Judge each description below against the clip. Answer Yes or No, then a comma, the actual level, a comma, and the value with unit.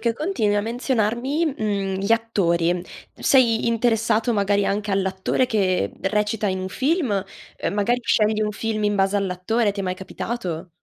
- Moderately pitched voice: No, high, 210 Hz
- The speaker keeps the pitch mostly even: No, average, 3.0 semitones